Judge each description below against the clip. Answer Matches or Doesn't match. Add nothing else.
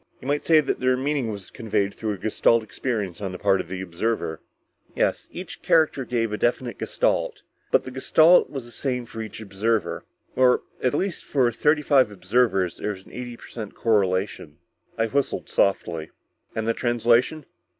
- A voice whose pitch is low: Matches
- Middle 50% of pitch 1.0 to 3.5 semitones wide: Doesn't match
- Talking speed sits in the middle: Matches